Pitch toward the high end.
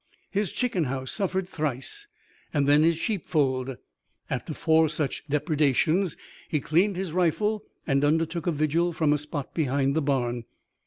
No: medium, 155 Hz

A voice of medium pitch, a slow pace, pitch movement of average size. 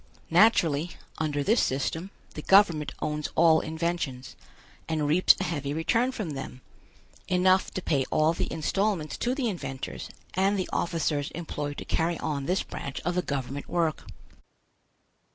No: medium, 160 Hz; average, 150 wpm; average, 4.0 semitones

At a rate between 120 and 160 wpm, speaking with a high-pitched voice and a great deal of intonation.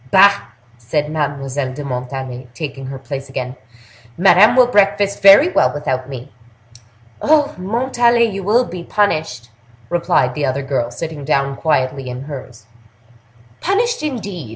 No: slow, 135 wpm; medium, 150 Hz; wide, 7.3 semitones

